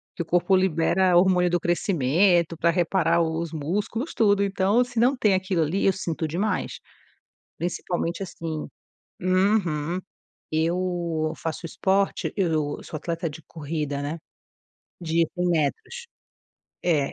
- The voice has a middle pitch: Yes, medium, 175 Hz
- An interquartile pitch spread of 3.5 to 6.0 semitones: No, average, 2.8 semitones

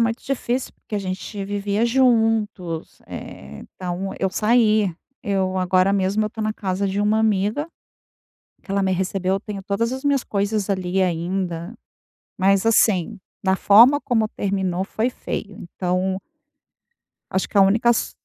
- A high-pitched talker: Yes, high, 200 Hz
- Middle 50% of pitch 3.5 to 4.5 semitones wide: No, average, 2.8 semitones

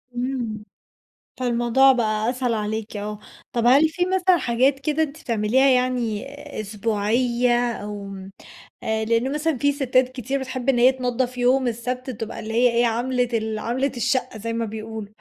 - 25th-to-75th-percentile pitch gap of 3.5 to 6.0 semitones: No, average, 2.8 semitones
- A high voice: Yes, high, 245 Hz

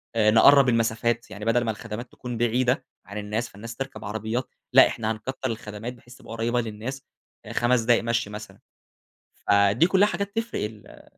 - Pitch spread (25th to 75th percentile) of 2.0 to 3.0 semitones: Yes, narrow, 2.4 semitones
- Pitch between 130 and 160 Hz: No, low, 115 Hz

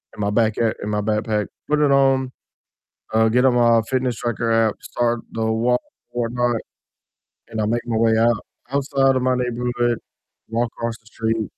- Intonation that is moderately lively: No, narrow, 1.7 semitones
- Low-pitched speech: Yes, low, 115 Hz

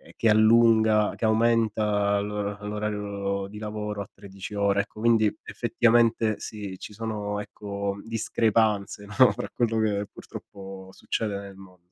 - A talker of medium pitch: No, low, 105 Hz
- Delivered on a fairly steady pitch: Yes, narrow, 1.5 semitones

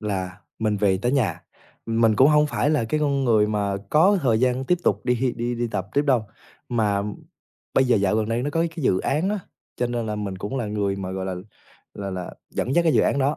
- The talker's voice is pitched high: No, low, 115 Hz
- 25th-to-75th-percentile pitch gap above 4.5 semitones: Yes, average, 5.2 semitones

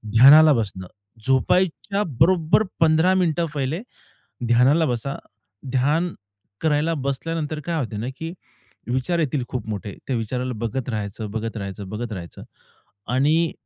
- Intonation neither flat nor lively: No, wide, 5.9 semitones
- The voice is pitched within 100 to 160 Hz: Yes, low, 135 Hz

